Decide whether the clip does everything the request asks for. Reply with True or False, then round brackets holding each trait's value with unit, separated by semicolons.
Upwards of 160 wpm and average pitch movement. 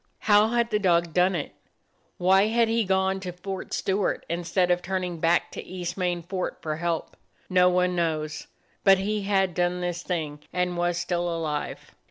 False (180 wpm; 1.9 semitones)